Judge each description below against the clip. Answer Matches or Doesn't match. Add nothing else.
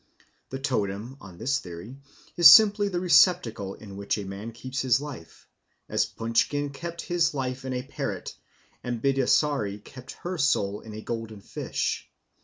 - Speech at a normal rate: Matches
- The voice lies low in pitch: Matches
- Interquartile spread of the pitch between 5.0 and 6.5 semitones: Matches